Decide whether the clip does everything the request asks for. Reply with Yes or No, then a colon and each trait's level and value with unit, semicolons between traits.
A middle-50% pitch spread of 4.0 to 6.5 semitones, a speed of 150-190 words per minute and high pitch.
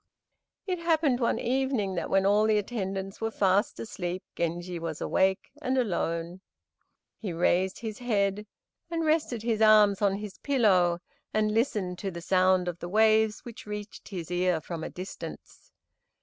No: average, 3.5 semitones; average, 160 wpm; high, 200 Hz